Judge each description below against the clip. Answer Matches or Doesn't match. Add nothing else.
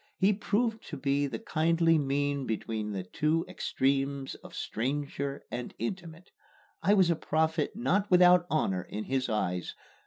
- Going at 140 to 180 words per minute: Matches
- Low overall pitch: Doesn't match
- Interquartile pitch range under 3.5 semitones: Doesn't match